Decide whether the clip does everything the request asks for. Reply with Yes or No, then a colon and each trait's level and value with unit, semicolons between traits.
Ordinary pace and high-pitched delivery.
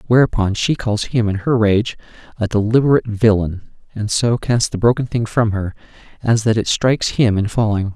No: average, 190 wpm; low, 110 Hz